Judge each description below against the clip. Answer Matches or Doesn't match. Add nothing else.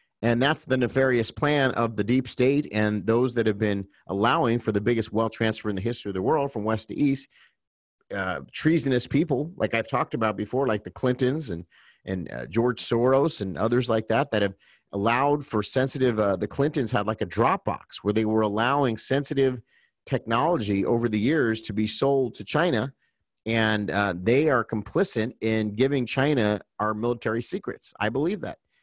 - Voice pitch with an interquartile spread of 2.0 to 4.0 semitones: Matches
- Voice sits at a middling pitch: Doesn't match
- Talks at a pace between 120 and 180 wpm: Doesn't match